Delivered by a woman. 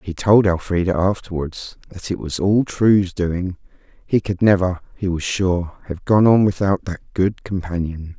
No: male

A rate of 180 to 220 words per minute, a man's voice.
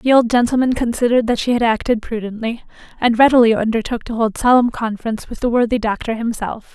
No: average, 185 wpm; female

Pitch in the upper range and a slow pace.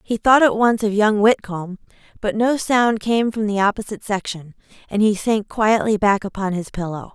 No: high, 210 Hz; average, 195 wpm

